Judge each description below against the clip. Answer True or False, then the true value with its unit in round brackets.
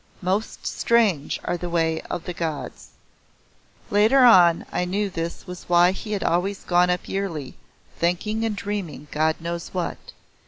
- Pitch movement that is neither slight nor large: True (3.1 semitones)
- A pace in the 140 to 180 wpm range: True (155 wpm)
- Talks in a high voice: False (180 Hz)